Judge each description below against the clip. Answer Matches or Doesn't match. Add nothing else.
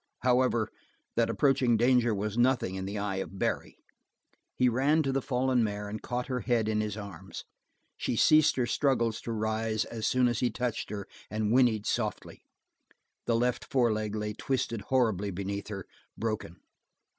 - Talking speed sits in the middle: Matches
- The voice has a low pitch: Matches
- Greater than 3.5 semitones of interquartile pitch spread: Doesn't match